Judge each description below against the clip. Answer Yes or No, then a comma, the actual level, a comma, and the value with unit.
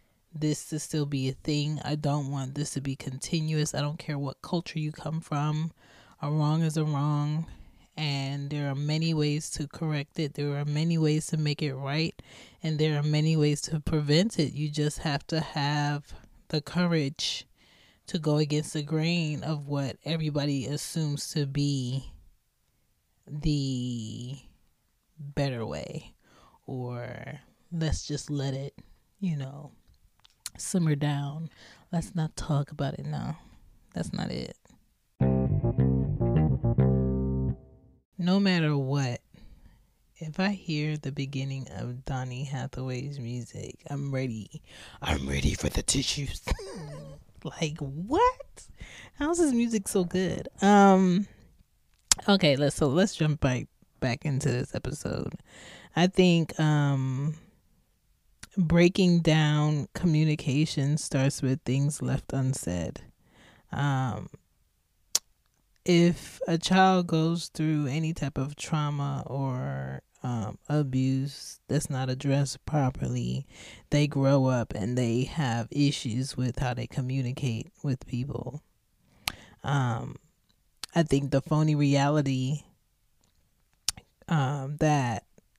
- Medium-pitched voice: Yes, medium, 145 Hz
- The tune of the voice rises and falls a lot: No, average, 3.0 semitones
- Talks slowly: Yes, slow, 125 wpm